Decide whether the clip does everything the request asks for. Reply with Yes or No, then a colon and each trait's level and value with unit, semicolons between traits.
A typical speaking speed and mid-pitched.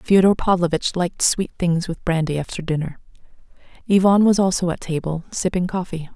Yes: average, 155 wpm; medium, 175 Hz